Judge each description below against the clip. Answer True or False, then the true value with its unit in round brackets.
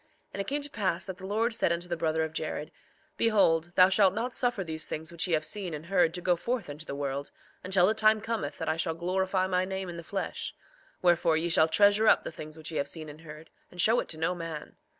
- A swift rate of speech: True (265 wpm)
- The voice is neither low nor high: True (175 Hz)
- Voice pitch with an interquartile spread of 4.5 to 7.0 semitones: False (3.7 semitones)